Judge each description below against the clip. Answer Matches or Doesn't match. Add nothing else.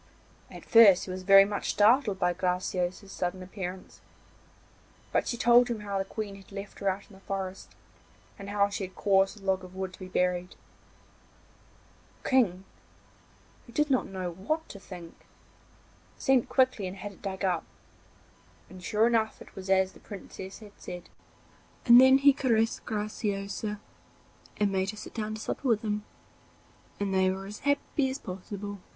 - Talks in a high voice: Matches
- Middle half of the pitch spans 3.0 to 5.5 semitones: Doesn't match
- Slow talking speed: Doesn't match